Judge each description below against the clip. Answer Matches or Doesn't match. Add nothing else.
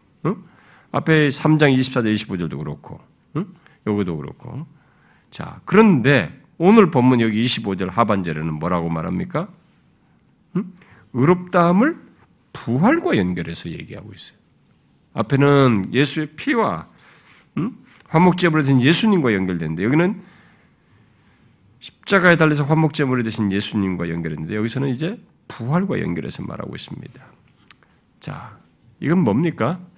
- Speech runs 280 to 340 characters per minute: Doesn't match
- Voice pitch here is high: Doesn't match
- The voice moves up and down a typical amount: Doesn't match